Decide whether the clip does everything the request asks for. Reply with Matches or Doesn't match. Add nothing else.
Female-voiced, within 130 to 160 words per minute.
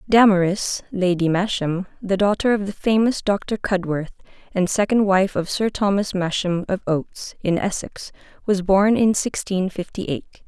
Matches